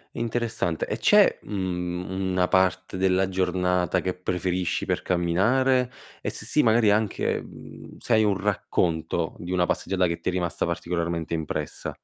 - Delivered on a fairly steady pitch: Yes, narrow, 2.3 semitones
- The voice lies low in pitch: Yes, very low, 90 Hz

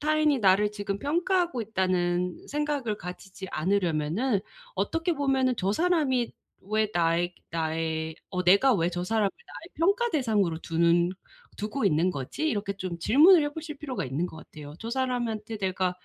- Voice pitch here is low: No, high, 205 Hz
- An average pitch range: No, wide, 7.7 semitones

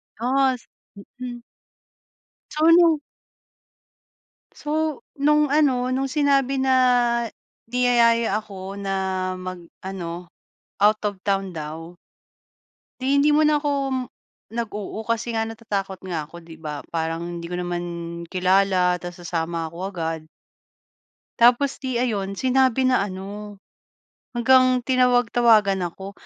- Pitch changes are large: Yes, wide, 5.9 semitones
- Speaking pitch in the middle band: No, high, 215 Hz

